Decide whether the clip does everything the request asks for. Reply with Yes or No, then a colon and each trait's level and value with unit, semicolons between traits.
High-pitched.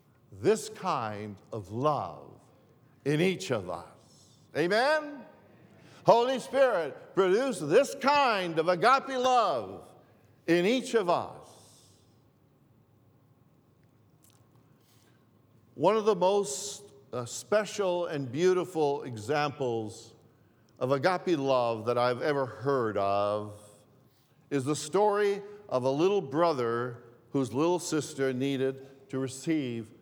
No: low, 135 Hz